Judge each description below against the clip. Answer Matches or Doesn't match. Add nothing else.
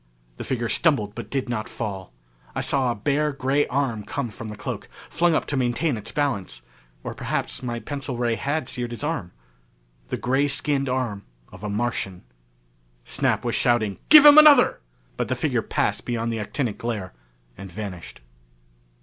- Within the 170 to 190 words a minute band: Matches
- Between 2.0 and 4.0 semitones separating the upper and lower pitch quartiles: Doesn't match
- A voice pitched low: Matches